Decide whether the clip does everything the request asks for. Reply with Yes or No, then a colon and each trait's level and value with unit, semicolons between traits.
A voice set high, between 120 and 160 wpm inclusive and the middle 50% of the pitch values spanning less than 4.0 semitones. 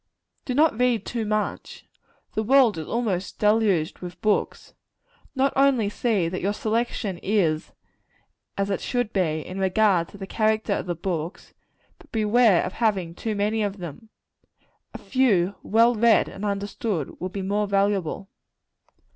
Yes: high, 205 Hz; average, 155 wpm; average, 3.2 semitones